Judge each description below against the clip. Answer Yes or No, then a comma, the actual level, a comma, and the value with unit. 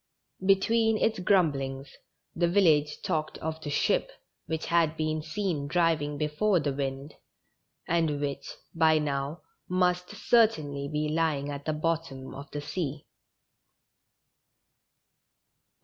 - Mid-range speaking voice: Yes, medium, 155 Hz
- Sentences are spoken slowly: Yes, slow, 115 wpm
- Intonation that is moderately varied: Yes, average, 3.4 semitones